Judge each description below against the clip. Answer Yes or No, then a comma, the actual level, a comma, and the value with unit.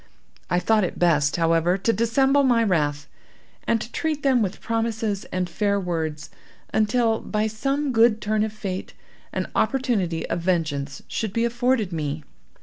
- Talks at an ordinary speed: Yes, average, 155 wpm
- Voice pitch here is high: Yes, high, 210 Hz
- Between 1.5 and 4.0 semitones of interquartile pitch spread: No, average, 5.2 semitones